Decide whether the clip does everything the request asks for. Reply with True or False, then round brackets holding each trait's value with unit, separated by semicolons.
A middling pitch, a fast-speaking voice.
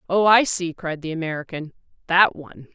False (170 Hz; 175 wpm)